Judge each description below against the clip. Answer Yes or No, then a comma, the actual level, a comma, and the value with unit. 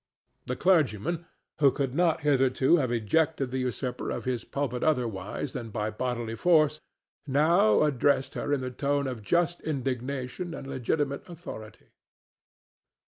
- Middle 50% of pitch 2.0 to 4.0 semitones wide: Yes, average, 3.7 semitones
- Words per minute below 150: Yes, average, 140 wpm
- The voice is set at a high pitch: No, low, 135 Hz